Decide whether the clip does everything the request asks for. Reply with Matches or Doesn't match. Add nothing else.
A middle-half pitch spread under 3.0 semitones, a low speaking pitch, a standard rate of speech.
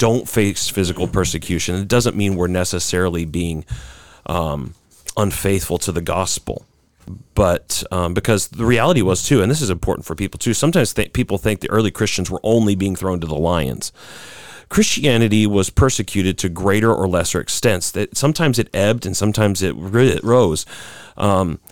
Doesn't match